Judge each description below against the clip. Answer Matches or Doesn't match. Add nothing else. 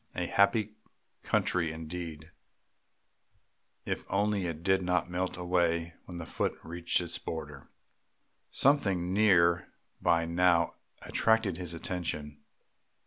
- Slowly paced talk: Matches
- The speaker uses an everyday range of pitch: Doesn't match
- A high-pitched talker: Doesn't match